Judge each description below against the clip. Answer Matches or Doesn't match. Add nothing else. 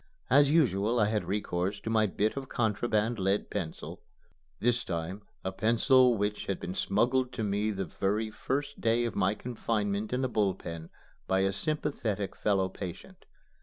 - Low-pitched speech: Matches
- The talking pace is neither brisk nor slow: Matches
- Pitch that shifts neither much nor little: Matches